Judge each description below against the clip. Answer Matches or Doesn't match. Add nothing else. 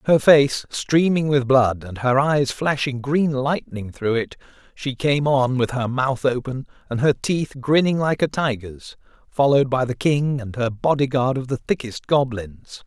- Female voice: Doesn't match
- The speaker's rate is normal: Matches